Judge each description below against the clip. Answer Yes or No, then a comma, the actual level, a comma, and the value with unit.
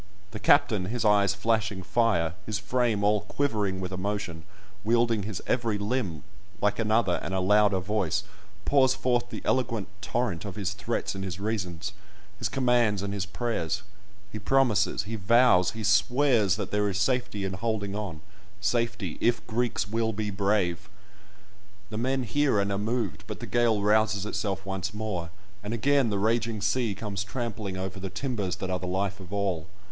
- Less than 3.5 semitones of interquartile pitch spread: Yes, average, 3.1 semitones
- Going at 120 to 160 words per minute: No, average, 170 wpm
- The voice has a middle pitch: No, low, 105 Hz